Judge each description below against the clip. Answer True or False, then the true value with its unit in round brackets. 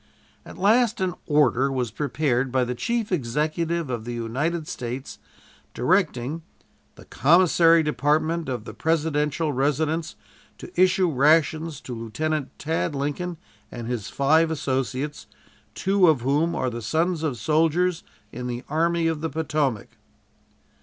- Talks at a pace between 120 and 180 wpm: True (135 wpm)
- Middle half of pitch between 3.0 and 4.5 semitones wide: True (4.2 semitones)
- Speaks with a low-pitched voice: False (150 Hz)